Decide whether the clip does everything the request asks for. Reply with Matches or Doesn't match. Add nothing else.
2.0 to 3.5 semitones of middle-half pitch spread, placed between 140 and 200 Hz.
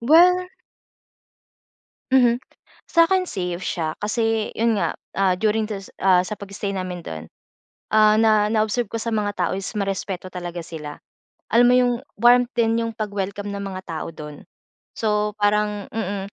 Doesn't match